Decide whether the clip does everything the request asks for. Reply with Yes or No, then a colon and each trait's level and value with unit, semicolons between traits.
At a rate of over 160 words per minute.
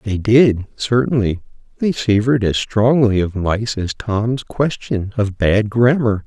No: average, 145 wpm